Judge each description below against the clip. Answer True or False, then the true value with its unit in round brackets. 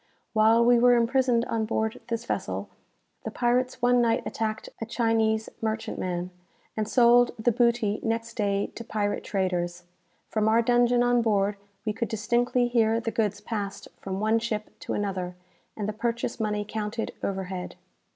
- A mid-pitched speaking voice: False (225 Hz)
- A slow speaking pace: False (160 wpm)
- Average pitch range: False (2.1 semitones)